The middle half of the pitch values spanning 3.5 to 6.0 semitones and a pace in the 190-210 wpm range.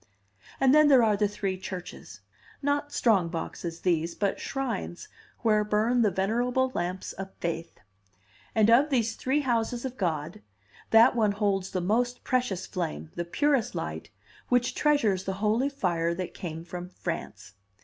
No: wide, 5.5 semitones; average, 155 wpm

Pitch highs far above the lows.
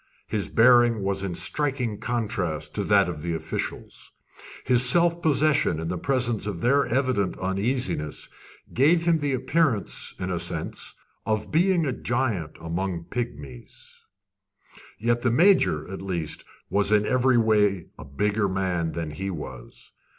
Yes: wide, 6.4 semitones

